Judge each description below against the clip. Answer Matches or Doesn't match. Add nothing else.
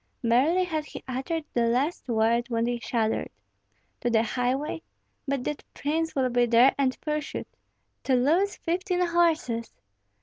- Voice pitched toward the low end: Doesn't match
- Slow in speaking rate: Doesn't match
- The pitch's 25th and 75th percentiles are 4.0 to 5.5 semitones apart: Matches